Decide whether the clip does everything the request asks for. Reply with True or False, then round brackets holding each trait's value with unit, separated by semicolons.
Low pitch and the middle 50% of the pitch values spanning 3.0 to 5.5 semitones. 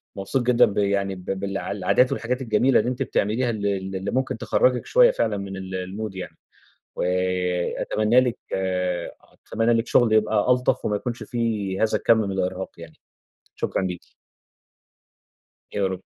True (105 Hz; 3.8 semitones)